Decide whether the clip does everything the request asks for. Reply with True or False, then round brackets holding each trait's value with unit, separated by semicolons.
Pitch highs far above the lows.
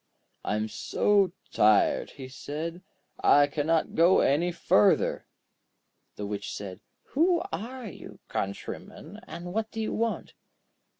True (8.4 semitones)